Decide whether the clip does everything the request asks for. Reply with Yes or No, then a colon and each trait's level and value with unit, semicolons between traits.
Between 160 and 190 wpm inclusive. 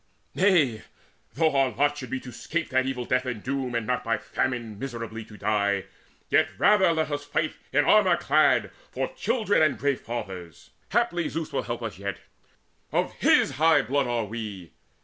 Yes: average, 180 wpm